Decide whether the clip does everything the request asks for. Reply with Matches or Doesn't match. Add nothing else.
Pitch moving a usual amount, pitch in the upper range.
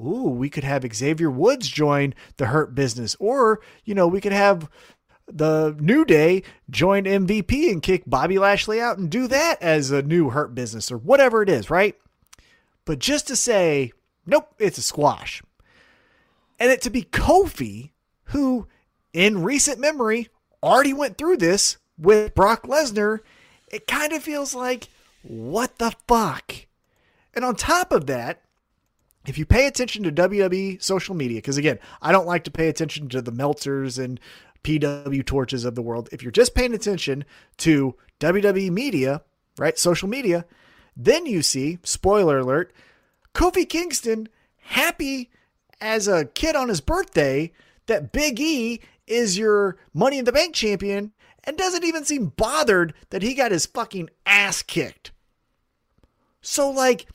Doesn't match